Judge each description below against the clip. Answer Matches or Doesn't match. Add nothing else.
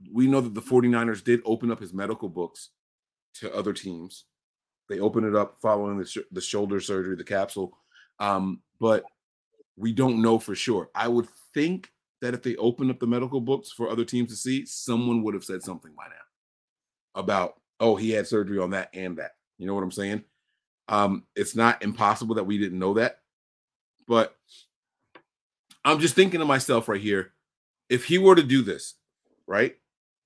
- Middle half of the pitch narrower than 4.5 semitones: Matches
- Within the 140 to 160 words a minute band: Doesn't match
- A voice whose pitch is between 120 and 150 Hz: Doesn't match